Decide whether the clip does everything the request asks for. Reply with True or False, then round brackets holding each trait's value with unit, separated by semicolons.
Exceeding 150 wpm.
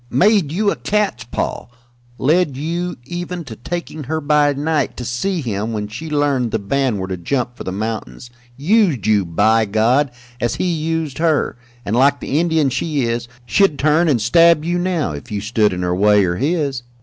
True (195 wpm)